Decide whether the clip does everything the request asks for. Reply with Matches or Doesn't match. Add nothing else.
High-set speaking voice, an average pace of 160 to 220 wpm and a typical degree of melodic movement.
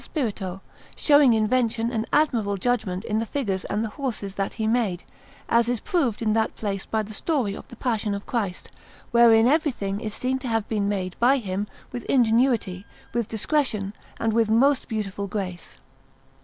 Matches